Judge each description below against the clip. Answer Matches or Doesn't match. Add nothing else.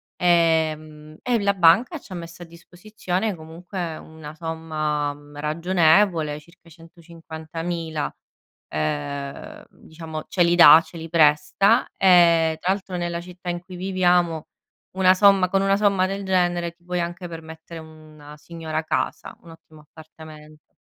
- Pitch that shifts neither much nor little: Doesn't match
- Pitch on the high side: Doesn't match